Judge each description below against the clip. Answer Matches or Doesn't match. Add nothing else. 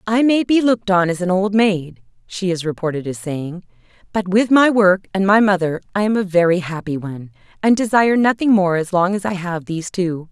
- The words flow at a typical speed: Doesn't match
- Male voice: Doesn't match